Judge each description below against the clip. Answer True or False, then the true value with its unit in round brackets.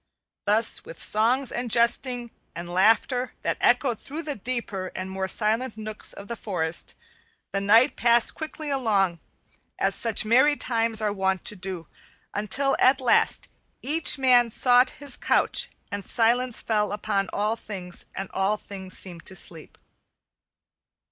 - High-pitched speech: True (220 Hz)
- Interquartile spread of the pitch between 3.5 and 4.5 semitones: True (4.2 semitones)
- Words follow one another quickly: False (150 wpm)